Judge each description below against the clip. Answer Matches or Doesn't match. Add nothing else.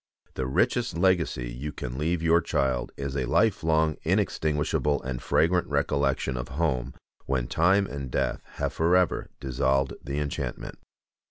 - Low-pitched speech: Matches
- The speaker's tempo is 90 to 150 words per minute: Matches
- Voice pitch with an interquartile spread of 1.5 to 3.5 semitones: Doesn't match